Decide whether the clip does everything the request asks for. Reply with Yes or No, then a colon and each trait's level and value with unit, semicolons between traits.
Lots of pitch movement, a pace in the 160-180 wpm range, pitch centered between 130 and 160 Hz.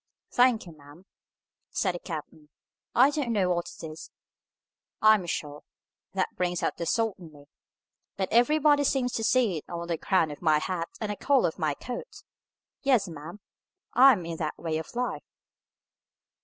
No: wide, 6.8 semitones; average, 175 wpm; medium, 185 Hz